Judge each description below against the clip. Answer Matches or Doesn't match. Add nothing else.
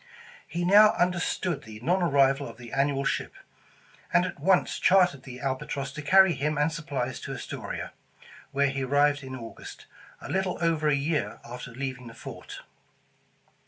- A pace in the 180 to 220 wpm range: Doesn't match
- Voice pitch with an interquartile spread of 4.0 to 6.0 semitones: Matches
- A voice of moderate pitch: Matches